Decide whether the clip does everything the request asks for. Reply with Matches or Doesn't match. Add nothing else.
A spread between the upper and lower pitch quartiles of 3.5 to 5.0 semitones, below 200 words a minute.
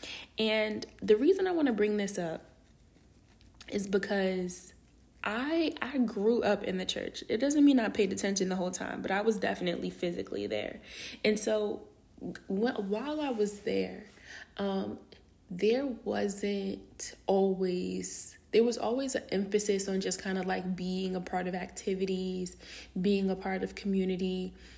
Doesn't match